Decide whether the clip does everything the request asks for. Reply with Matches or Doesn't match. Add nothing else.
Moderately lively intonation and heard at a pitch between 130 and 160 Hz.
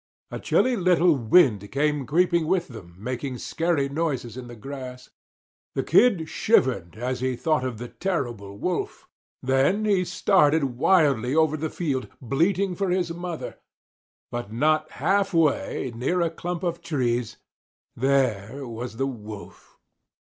Doesn't match